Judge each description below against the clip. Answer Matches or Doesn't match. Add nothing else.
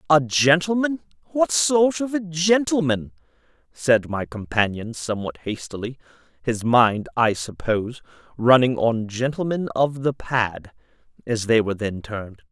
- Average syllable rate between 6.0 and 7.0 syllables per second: Doesn't match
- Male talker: Matches